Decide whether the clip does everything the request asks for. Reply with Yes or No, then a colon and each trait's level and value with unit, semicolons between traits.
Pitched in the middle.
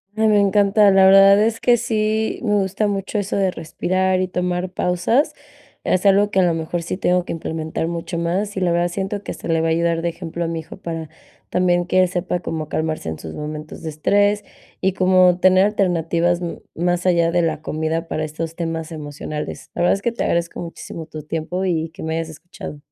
Yes: medium, 175 Hz